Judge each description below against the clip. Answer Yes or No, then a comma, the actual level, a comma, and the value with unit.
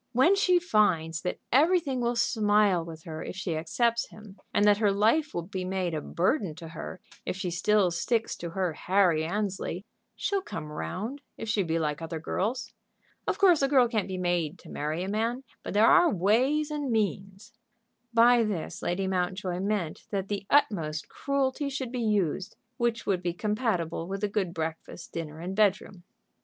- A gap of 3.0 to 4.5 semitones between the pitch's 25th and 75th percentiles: No, average, 5.1 semitones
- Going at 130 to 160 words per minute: No, average, 185 wpm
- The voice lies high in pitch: Yes, high, 200 Hz